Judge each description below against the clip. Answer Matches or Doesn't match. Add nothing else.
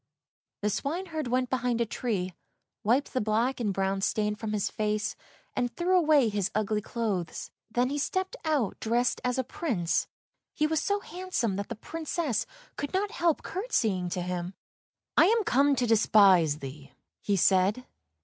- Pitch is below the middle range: Doesn't match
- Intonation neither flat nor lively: Doesn't match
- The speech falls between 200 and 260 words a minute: Doesn't match